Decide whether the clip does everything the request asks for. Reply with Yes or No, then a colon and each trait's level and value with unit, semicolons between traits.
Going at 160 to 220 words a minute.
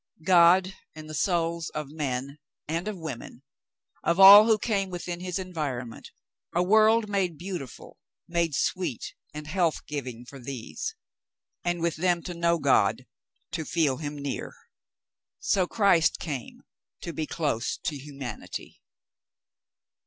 No: average, 145 wpm